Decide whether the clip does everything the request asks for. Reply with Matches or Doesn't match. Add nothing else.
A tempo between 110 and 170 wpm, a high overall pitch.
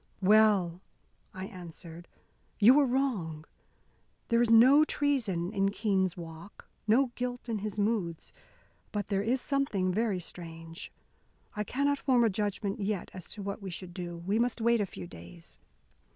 Matches